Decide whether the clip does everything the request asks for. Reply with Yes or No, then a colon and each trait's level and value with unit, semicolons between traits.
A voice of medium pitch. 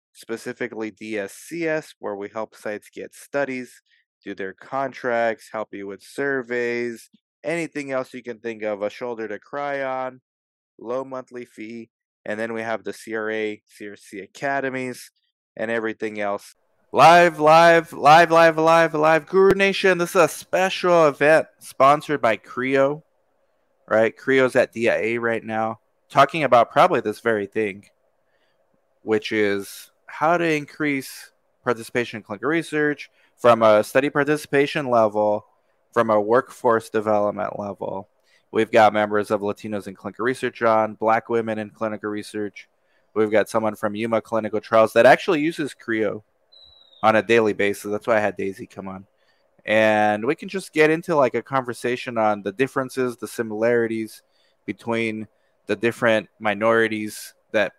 No: low, 115 Hz